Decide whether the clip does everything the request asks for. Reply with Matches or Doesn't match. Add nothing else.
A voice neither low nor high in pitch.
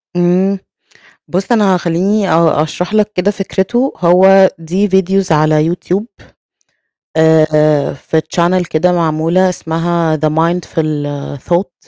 Matches